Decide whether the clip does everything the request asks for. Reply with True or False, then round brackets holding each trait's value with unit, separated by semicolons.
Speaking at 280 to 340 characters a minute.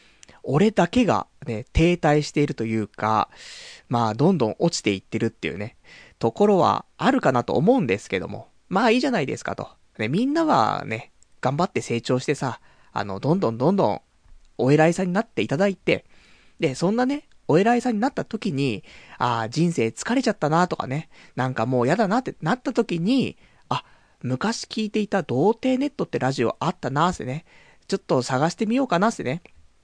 False (370 characters per minute)